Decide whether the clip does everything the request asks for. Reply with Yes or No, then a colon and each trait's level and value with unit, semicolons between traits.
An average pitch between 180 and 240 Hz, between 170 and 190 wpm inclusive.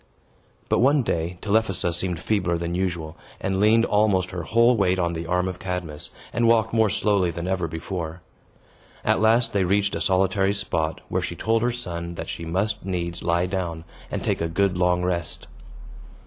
No: very low, 95 Hz; average, 185 wpm